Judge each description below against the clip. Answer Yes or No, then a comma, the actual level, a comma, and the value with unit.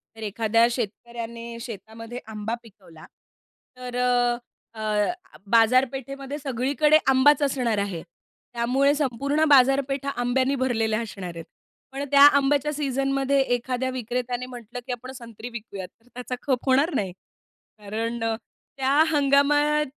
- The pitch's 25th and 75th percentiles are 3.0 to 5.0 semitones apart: Yes, average, 3.3 semitones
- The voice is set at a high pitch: Yes, very high, 250 Hz